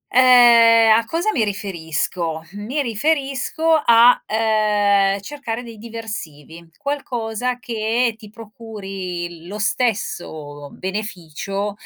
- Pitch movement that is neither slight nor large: Yes, average, 3.5 semitones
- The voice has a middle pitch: No, high, 220 Hz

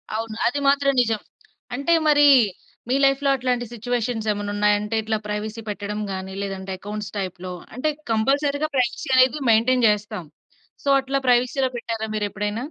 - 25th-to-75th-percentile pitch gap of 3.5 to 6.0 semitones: Yes, average, 3.9 semitones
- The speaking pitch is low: No, high, 225 Hz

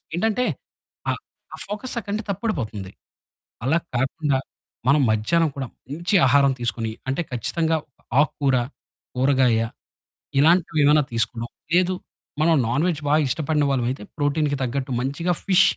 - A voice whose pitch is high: No, medium, 145 Hz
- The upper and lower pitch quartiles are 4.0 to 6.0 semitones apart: Yes, average, 4.6 semitones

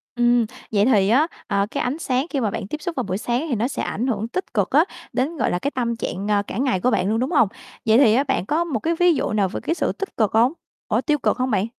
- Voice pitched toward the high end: Yes, high, 245 Hz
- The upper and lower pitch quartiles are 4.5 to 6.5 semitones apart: Yes, average, 4.8 semitones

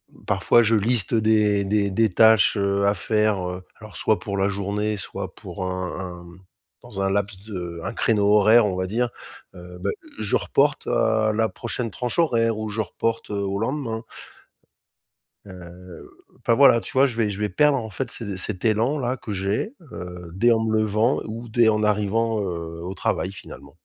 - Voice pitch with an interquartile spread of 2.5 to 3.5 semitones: Yes, average, 2.9 semitones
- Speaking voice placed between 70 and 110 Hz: Yes, low, 105 Hz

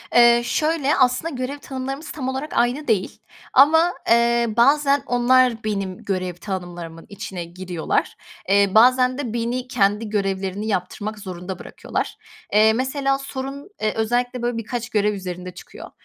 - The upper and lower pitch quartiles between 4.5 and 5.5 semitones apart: Yes, average, 4.8 semitones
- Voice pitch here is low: No, high, 235 Hz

